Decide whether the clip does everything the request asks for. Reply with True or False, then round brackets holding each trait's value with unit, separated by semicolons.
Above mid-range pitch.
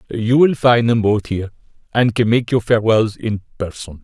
False (115 Hz)